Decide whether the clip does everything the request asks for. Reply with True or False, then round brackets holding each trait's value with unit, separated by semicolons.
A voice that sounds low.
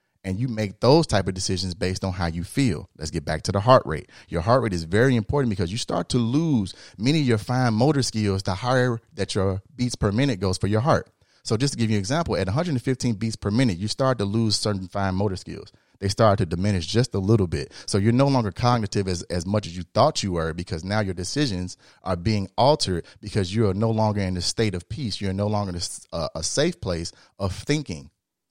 True (105 Hz)